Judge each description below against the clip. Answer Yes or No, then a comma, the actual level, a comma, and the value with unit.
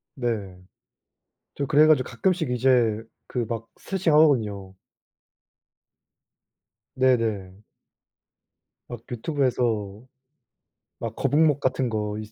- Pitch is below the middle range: Yes, low, 120 Hz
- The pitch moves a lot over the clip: No, average, 4.5 semitones